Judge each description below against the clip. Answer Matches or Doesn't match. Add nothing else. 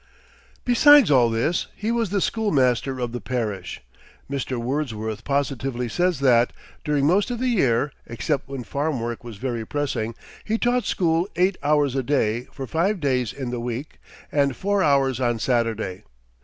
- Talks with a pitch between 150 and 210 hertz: Doesn't match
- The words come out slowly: Doesn't match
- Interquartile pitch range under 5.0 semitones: Doesn't match